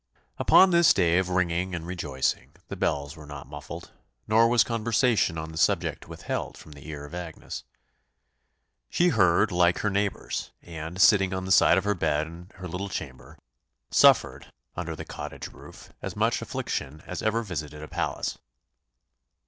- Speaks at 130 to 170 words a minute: Yes, average, 165 wpm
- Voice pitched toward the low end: Yes, very low, 90 Hz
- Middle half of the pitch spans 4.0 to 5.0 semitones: Yes, average, 4.4 semitones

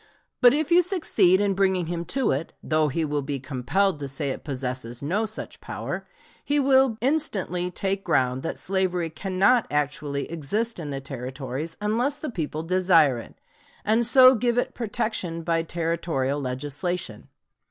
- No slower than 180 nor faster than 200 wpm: No, average, 160 wpm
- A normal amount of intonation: No, wide, 7.1 semitones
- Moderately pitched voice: Yes, medium, 170 Hz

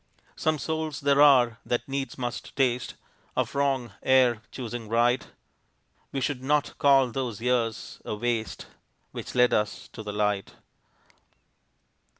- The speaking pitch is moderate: No, low, 125 Hz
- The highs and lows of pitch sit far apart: No, average, 2.9 semitones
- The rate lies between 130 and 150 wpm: Yes, slow, 135 wpm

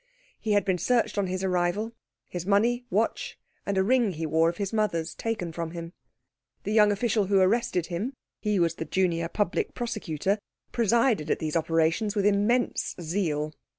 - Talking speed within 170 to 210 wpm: Yes, average, 175 wpm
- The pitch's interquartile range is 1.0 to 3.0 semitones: No, average, 4.3 semitones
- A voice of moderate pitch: No, high, 195 Hz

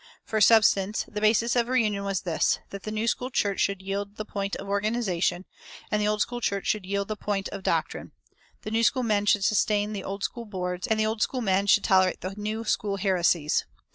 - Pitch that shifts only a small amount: Yes, narrow, 1.8 semitones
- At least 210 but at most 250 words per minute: Yes, fast, 220 wpm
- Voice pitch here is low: No, high, 205 Hz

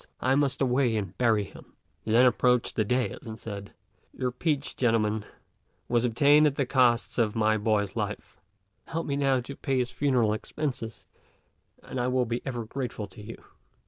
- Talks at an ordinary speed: Yes, average, 175 wpm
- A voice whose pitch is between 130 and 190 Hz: No, low, 120 Hz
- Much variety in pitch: No, average, 3.3 semitones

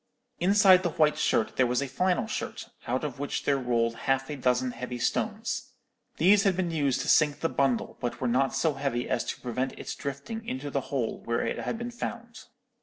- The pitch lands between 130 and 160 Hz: Yes, medium, 140 Hz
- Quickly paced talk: Yes, fast, 210 wpm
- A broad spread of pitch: Yes, wide, 6.2 semitones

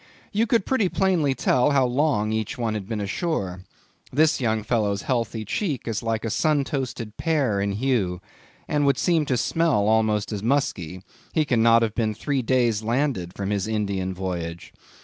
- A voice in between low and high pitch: No, low, 115 Hz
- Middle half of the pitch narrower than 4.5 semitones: No, wide, 5.4 semitones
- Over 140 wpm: Yes, average, 175 wpm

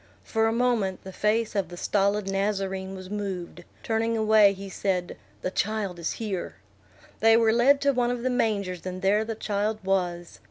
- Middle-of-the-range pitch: No, high, 205 Hz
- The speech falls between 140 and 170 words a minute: No, average, 185 wpm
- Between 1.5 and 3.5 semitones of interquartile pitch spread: Yes, average, 2.8 semitones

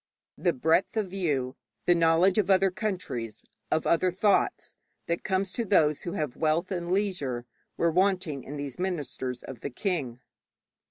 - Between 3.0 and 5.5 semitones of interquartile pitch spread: Yes, average, 4.9 semitones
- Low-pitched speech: No, medium, 170 Hz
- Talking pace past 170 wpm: No, average, 160 wpm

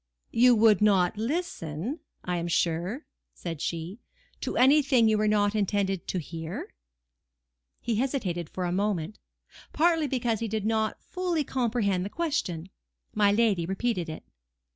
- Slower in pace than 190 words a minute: Yes, average, 140 wpm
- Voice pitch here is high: Yes, high, 210 Hz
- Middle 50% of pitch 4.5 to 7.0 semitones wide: Yes, average, 5.3 semitones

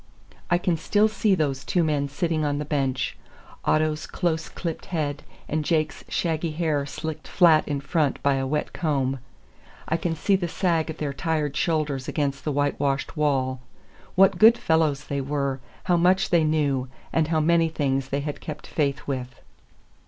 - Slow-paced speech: No, average, 175 wpm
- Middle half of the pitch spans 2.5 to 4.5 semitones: Yes, average, 2.8 semitones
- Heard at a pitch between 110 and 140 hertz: No, medium, 155 Hz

